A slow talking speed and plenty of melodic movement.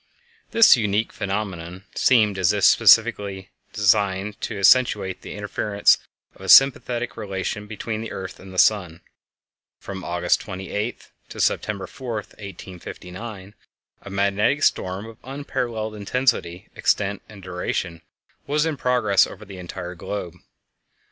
No: slow, 130 wpm; average, 2.8 semitones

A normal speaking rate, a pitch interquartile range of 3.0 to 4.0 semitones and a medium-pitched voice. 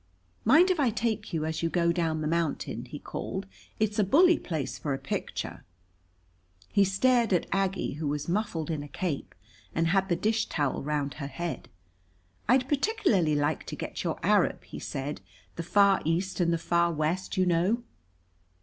No: average, 180 wpm; average, 5.0 semitones; medium, 175 Hz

